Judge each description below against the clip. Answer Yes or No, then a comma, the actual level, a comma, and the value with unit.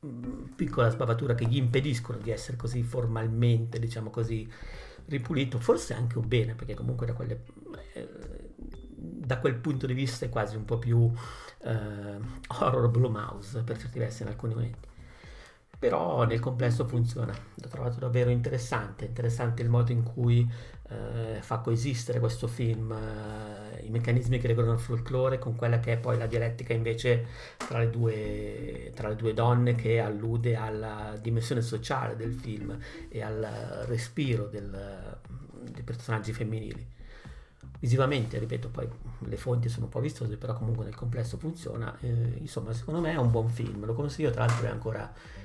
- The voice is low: Yes, low, 120 Hz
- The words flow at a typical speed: Yes, average, 160 wpm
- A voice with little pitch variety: Yes, narrow, 1.5 semitones